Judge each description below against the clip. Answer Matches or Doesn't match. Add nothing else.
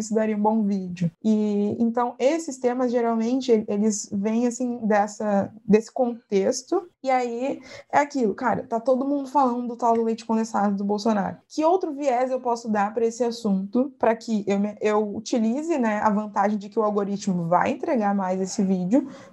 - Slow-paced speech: Doesn't match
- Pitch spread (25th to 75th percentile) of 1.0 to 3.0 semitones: Doesn't match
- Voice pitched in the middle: Doesn't match